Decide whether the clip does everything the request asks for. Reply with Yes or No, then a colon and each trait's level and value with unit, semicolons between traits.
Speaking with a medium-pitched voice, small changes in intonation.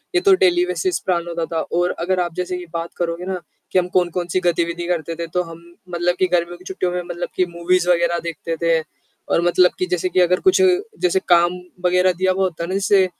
Yes: medium, 180 Hz; narrow, 1.3 semitones